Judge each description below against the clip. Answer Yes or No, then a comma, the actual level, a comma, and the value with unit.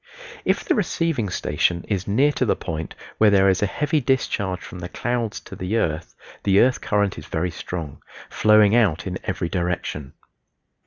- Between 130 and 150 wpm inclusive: No, average, 175 wpm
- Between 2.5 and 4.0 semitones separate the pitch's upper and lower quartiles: No, average, 4.6 semitones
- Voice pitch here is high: No, low, 100 Hz